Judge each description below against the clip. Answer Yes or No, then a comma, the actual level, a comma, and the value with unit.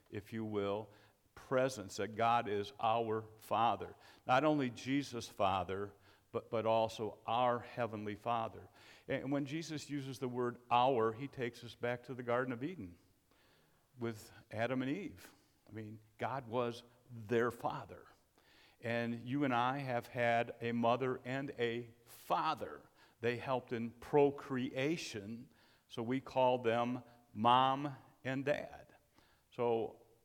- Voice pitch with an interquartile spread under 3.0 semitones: Yes, narrow, 2.5 semitones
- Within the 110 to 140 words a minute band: Yes, slow, 135 wpm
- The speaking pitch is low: Yes, low, 120 Hz